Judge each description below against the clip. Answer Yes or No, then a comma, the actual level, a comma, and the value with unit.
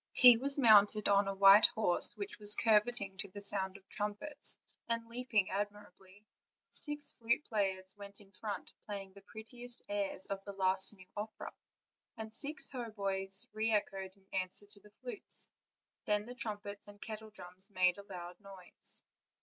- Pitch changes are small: Yes, narrow, 2.2 semitones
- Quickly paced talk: No, average, 165 wpm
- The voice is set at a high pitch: Yes, high, 205 Hz